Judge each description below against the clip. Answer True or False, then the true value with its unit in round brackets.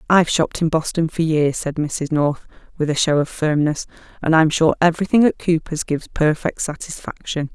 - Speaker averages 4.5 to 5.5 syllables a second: True (5.4 syllables/s)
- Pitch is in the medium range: True (160 Hz)